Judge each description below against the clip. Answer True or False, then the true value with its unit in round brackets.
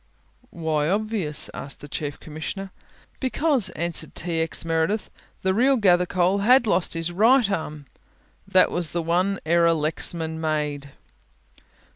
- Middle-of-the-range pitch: True (170 Hz)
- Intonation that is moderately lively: True (3.8 semitones)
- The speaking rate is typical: False (130 wpm)